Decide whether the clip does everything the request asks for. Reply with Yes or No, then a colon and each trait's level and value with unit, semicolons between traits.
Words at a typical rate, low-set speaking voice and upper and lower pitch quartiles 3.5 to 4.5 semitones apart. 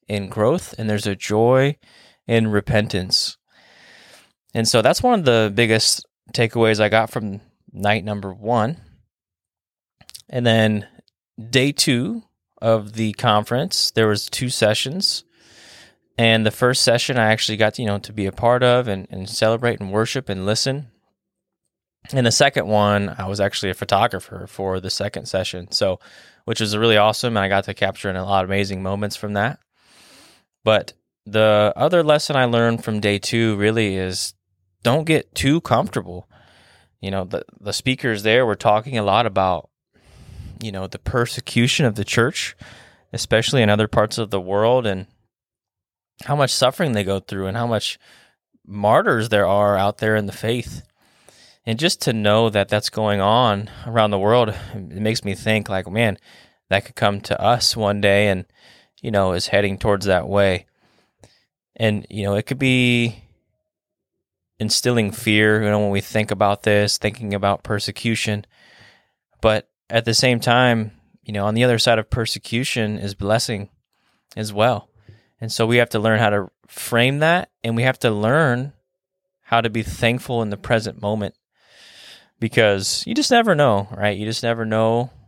No: average, 170 wpm; low, 110 Hz; average, 2.8 semitones